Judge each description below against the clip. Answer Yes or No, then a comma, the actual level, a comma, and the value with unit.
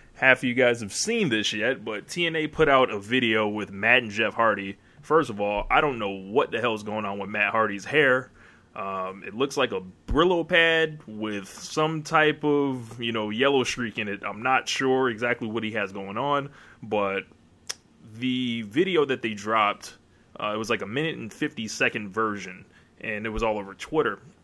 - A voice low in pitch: Yes, low, 115 Hz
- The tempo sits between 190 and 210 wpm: Yes, fast, 205 wpm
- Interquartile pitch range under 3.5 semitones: No, average, 4.0 semitones